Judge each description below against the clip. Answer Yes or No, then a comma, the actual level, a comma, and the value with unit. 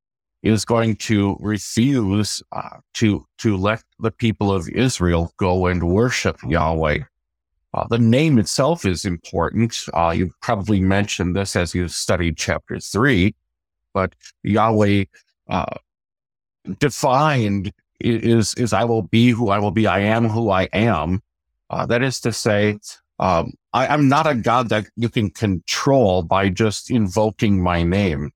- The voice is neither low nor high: No, low, 105 Hz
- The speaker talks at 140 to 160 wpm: Yes, average, 150 wpm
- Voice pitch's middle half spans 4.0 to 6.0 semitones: Yes, average, 4.3 semitones